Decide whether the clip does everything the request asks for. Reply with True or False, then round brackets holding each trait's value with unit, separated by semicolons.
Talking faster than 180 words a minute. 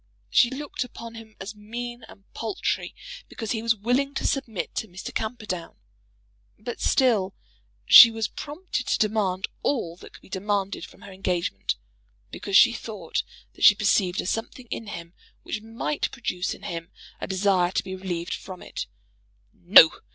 False (165 wpm)